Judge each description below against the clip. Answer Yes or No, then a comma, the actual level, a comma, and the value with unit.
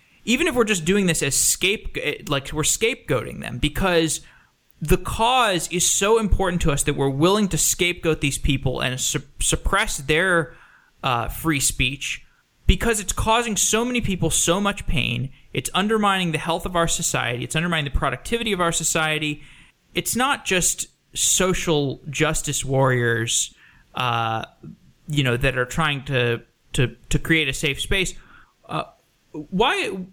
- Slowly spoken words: No, average, 155 wpm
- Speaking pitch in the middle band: Yes, medium, 160 Hz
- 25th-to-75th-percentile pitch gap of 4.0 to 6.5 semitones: Yes, average, 5.2 semitones